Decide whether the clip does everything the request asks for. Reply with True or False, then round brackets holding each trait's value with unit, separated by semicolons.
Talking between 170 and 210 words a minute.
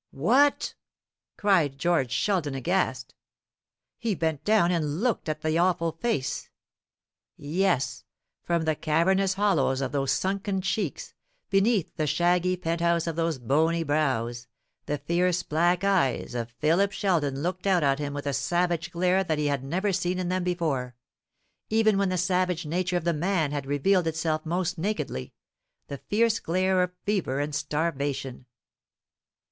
False (150 wpm)